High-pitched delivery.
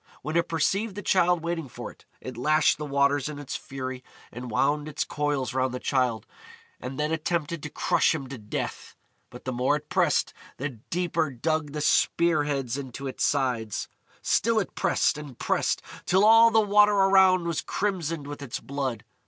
No: medium, 150 Hz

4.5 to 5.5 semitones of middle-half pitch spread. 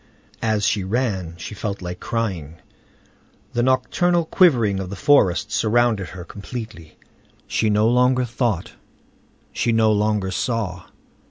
No: average, 4.1 semitones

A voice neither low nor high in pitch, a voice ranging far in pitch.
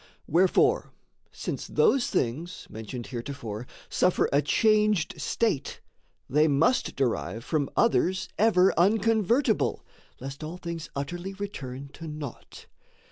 Yes: medium, 165 Hz; wide, 6.9 semitones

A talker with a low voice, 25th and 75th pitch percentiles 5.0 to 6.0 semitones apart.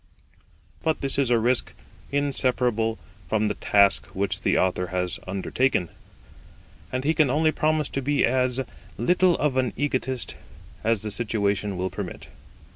Yes: low, 125 Hz; wide, 5.4 semitones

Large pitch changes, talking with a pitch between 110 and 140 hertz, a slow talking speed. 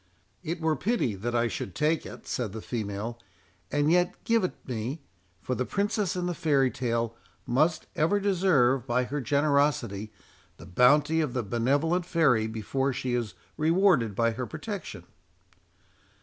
No: wide, 5.8 semitones; low, 135 Hz; average, 150 wpm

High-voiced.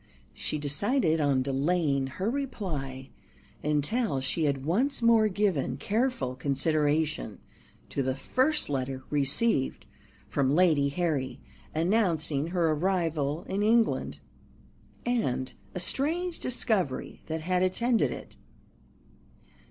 No: medium, 160 Hz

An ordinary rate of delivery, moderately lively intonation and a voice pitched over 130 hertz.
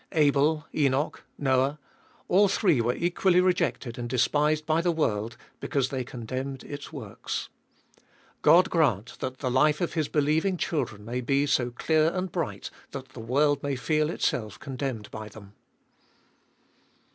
Yes: average, 155 wpm; average, 4.1 semitones; medium, 140 Hz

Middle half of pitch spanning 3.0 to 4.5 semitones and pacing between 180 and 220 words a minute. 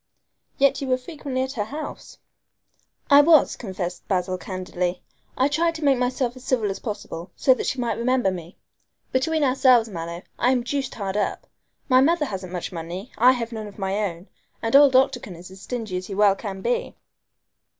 No: wide, 5.5 semitones; average, 190 wpm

